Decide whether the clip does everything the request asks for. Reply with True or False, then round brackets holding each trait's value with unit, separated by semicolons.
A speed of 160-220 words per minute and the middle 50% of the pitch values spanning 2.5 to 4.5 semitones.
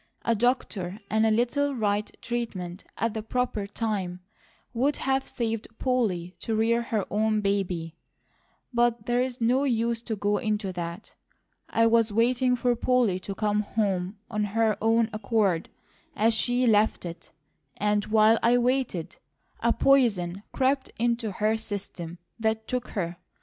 False (145 wpm; 2.9 semitones)